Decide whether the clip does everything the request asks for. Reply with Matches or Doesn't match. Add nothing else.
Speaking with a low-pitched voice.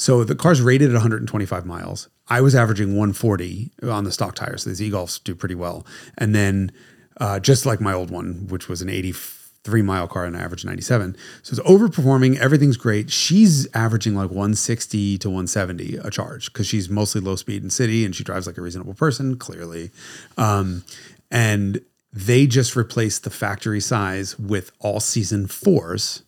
Matches